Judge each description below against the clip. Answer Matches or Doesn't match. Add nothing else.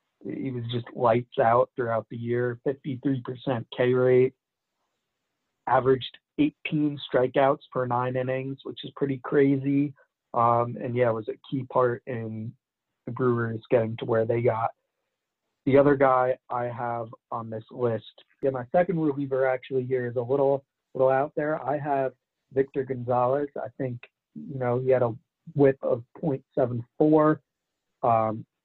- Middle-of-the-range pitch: Doesn't match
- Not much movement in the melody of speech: Matches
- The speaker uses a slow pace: Doesn't match